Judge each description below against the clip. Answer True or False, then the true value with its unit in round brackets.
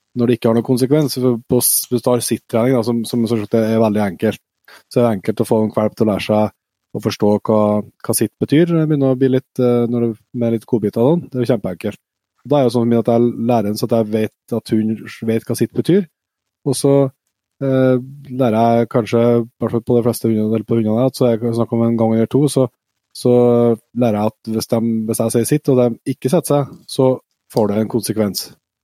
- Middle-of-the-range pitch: False (120 Hz)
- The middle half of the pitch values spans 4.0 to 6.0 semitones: False (2.4 semitones)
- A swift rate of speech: True (240 wpm)